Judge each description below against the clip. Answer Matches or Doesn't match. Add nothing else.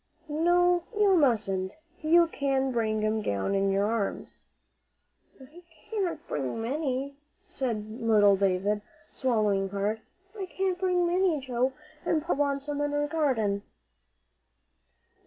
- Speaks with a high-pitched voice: Matches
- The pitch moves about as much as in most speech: Doesn't match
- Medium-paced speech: Doesn't match